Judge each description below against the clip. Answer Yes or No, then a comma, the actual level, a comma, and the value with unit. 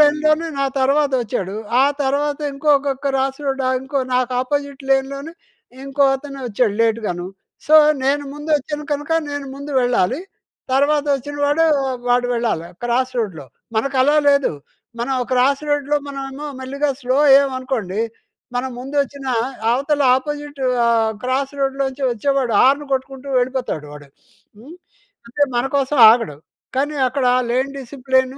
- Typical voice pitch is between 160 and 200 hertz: No, very high, 270 Hz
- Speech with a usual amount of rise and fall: No, narrow, 2.3 semitones